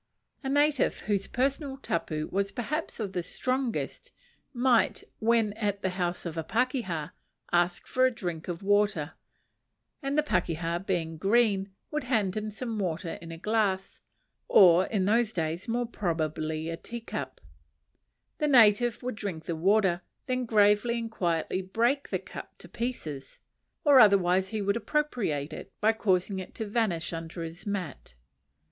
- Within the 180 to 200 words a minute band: No, average, 160 wpm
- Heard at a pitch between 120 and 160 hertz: No, high, 205 Hz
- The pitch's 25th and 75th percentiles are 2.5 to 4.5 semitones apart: No, wide, 5.4 semitones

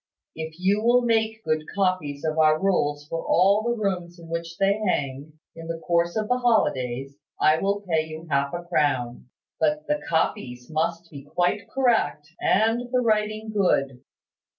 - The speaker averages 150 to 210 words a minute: Yes, average, 170 wpm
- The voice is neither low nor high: Yes, medium, 170 Hz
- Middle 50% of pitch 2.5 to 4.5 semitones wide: No, wide, 5.6 semitones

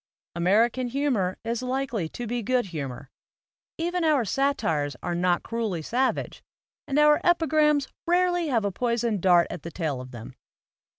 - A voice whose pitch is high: Yes, high, 235 Hz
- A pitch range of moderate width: No, wide, 8.1 semitones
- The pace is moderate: Yes, average, 155 wpm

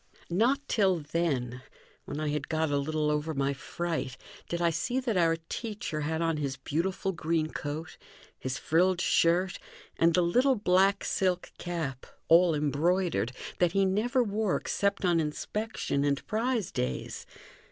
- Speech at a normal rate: Yes, average, 150 wpm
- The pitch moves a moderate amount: Yes, average, 4.2 semitones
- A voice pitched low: No, medium, 170 Hz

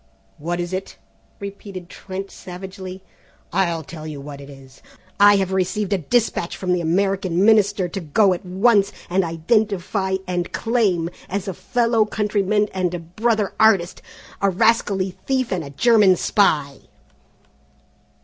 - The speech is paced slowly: No, average, 145 wpm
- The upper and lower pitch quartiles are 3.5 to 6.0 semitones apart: No, average, 2.9 semitones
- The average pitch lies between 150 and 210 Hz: Yes, high, 190 Hz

